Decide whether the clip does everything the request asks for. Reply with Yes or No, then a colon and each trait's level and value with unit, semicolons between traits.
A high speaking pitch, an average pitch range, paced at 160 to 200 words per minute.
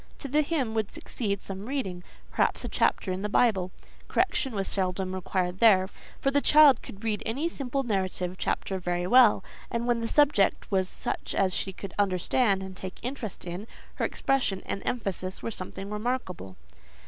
Yes: high, 200 Hz; average, 4.7 semitones; average, 175 wpm